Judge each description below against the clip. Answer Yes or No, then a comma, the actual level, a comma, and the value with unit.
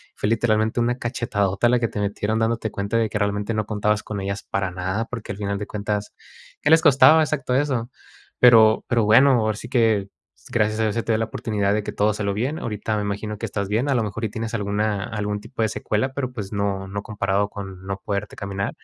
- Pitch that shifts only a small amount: Yes, narrow, 2.2 semitones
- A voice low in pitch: Yes, low, 105 Hz